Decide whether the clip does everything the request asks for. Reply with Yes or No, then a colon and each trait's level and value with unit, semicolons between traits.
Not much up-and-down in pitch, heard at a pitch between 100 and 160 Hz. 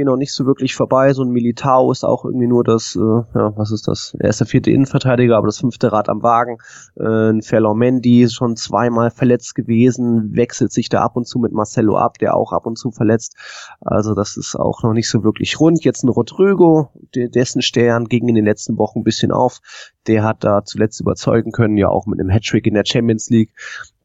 Yes: narrow, 2.2 semitones; low, 115 Hz